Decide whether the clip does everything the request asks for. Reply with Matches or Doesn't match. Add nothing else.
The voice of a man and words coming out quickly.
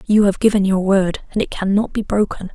Doesn't match